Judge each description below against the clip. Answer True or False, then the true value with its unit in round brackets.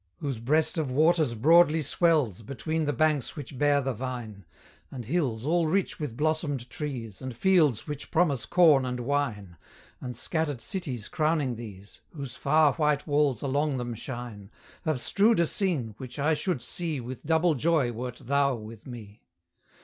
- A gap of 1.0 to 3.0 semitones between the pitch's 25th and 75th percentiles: False (4.4 semitones)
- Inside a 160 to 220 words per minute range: True (165 wpm)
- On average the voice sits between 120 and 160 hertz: True (140 Hz)